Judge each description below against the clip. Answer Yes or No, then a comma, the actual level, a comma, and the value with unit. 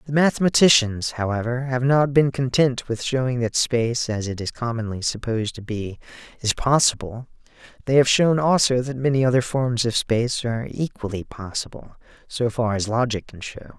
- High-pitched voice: No, low, 120 Hz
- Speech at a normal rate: Yes, average, 170 wpm